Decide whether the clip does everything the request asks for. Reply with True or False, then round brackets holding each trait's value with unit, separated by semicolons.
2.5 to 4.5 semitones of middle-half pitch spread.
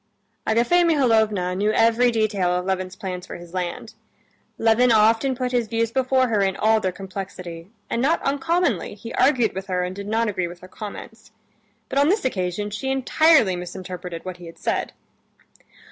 False (5.1 semitones)